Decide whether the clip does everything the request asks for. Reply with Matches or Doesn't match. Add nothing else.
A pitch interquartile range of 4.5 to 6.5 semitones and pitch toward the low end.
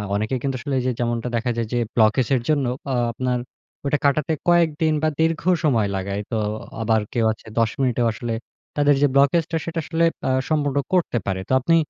Matches